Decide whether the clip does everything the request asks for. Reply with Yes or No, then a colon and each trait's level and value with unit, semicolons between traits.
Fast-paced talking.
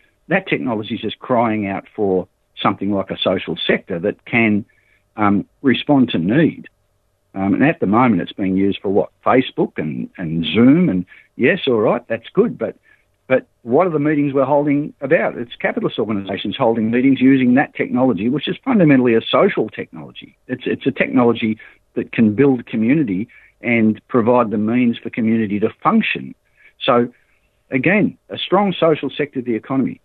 No: average, 170 wpm